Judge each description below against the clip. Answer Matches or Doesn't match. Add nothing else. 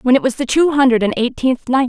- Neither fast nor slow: Doesn't match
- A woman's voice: Matches